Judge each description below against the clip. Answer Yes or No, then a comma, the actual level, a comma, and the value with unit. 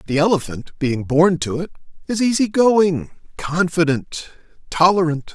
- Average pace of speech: No, slow, 125 wpm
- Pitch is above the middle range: No, medium, 170 Hz